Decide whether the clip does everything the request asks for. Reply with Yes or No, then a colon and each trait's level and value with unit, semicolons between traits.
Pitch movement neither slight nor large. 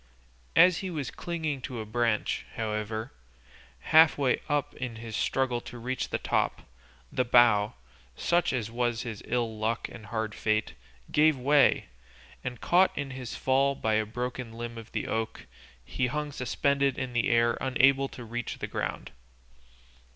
Yes: average, 3.3 semitones